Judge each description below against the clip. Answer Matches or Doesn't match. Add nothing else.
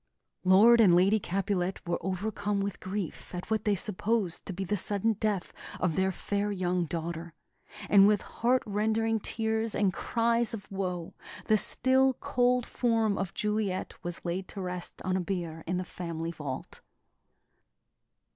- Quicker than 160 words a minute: Doesn't match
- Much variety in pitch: Doesn't match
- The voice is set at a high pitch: Matches